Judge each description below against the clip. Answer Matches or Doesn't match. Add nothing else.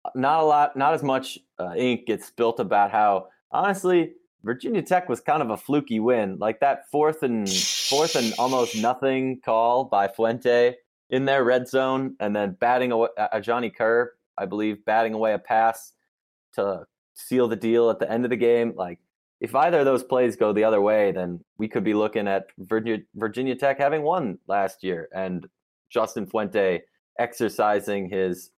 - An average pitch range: Matches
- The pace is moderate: Matches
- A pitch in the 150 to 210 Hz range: Doesn't match